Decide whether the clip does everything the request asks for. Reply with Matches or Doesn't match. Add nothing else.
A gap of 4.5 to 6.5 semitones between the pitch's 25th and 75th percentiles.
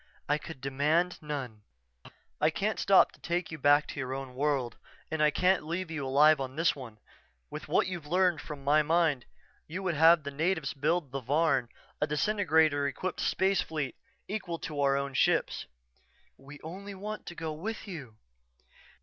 Doesn't match